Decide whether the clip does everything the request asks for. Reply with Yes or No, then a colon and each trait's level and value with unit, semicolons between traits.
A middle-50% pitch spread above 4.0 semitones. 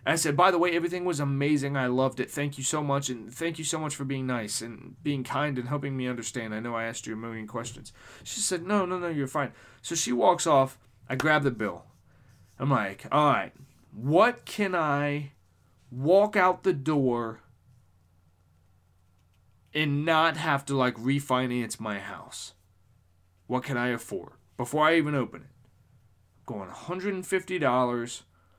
Yes: average, 5.1 semitones